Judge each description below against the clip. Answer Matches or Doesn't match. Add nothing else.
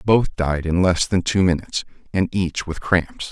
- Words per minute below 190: Doesn't match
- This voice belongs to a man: Matches